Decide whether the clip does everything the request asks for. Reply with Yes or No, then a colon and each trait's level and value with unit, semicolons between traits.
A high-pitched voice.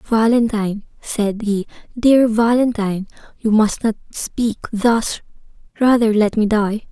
Yes: high, 220 Hz